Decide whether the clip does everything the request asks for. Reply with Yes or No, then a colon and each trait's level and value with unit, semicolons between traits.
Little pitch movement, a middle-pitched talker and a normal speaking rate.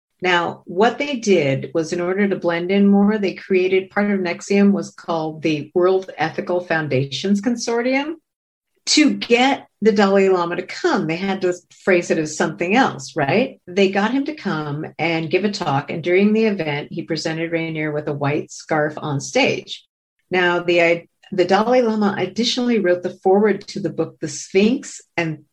No: average, 3.5 semitones; medium, 180 Hz; average, 180 wpm